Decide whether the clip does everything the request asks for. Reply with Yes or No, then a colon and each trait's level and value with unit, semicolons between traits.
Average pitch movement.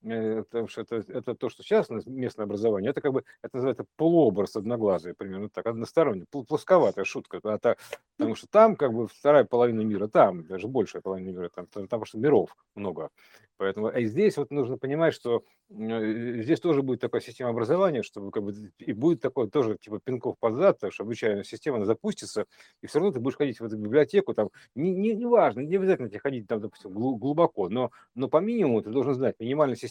No: wide, 5.9 semitones